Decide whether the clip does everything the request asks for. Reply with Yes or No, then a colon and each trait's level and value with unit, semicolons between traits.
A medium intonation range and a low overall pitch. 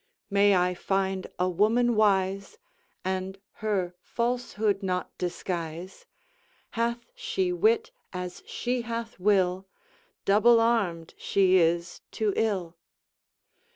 No: average, 4.2 semitones; high, 195 Hz